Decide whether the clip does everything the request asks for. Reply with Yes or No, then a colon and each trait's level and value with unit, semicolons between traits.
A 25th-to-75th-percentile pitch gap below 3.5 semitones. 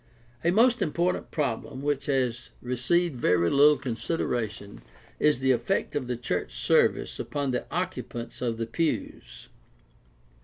No: average, 4.2 semitones